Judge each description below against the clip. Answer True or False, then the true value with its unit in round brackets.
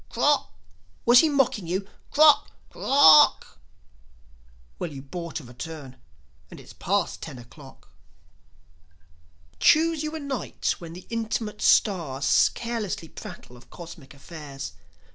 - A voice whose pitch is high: False (175 Hz)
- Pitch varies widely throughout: True (8.7 semitones)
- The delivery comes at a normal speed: False (125 wpm)